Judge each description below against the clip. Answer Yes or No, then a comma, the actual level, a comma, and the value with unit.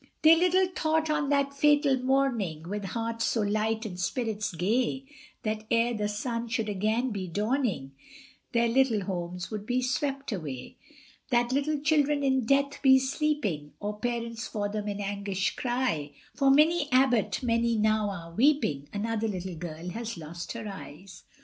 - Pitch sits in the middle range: No, high, 225 Hz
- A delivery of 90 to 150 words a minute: No, average, 160 wpm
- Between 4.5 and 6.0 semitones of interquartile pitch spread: Yes, average, 5.0 semitones